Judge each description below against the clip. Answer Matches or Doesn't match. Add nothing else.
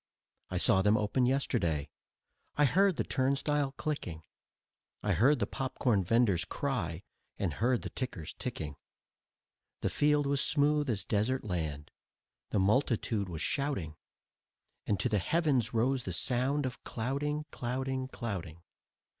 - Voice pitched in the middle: Doesn't match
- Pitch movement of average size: Doesn't match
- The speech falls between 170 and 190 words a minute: Doesn't match